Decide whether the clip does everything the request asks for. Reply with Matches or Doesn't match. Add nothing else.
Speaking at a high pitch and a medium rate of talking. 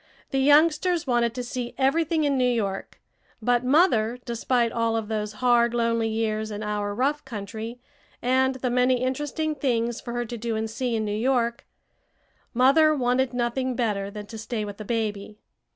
Matches